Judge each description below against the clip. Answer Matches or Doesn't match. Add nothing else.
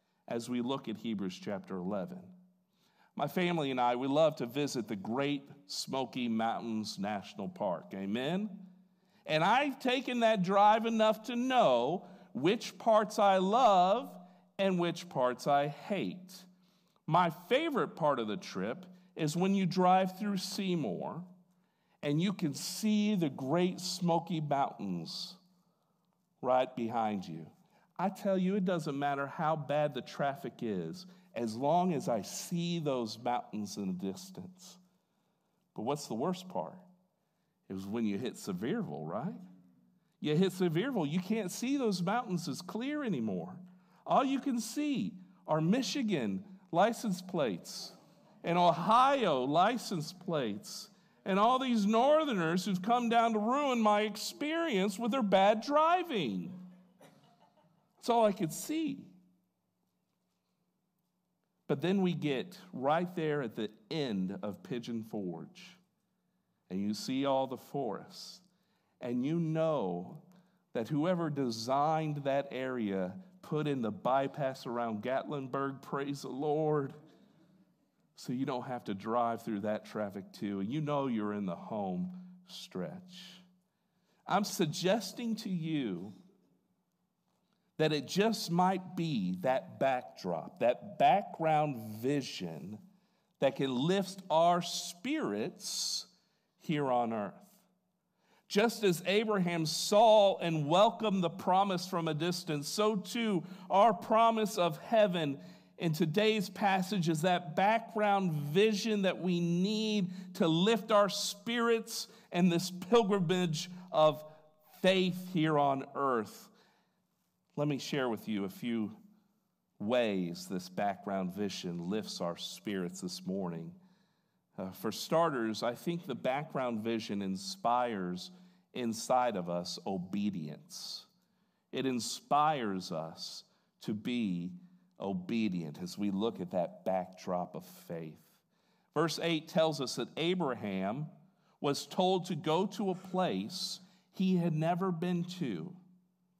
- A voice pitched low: Doesn't match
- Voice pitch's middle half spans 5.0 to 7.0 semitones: Matches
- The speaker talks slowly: Matches